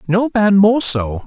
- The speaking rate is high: No, average, 190 wpm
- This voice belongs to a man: Yes, male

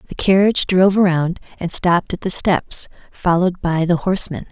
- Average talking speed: Yes, average, 175 wpm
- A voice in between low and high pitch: Yes, medium, 180 Hz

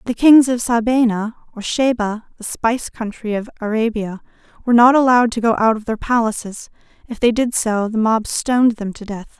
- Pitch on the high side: Yes, high, 230 Hz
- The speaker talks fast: No, average, 190 wpm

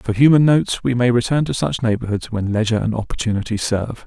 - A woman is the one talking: No, male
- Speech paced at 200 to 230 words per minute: Yes, fast, 205 wpm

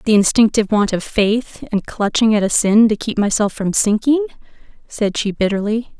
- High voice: Yes, high, 215 Hz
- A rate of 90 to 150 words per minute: No, average, 180 wpm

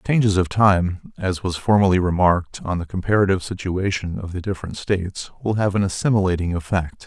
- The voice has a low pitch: Yes, very low, 95 Hz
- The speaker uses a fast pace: No, average, 180 wpm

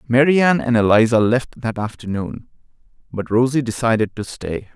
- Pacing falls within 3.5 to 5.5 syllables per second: Yes, 5.4 syllables/s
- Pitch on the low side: Yes, low, 120 Hz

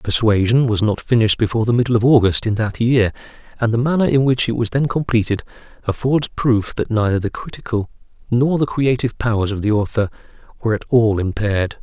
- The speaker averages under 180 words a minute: No, average, 195 wpm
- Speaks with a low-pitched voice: Yes, low, 115 Hz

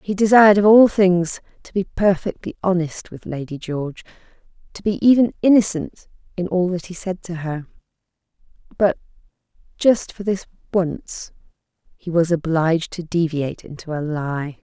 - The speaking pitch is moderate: Yes, medium, 180 Hz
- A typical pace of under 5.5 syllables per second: Yes, 4.9 syllables/s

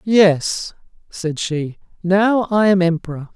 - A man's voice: Yes, male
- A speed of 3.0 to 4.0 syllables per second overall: Yes, 3.5 syllables/s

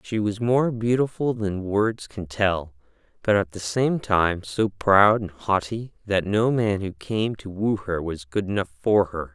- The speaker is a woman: No, male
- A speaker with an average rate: Yes, average, 195 wpm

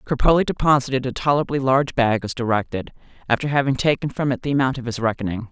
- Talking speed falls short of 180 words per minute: No, average, 195 wpm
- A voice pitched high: No, low, 130 Hz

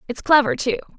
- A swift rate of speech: No, average, 185 wpm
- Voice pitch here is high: Yes, high, 235 Hz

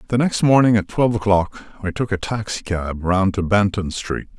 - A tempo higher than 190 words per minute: Yes, fast, 205 wpm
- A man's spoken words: Yes, male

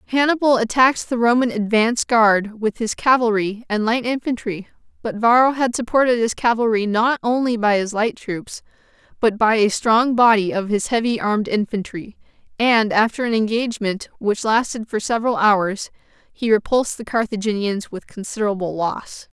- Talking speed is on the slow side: No, average, 155 wpm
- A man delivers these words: No, female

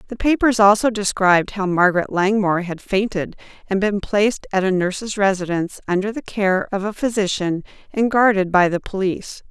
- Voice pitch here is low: No, high, 200 Hz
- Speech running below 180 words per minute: Yes, average, 170 wpm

